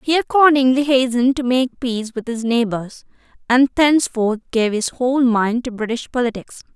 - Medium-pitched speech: No, high, 245 Hz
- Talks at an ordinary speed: Yes, average, 160 wpm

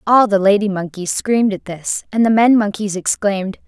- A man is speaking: No, female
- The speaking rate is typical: Yes, average, 195 wpm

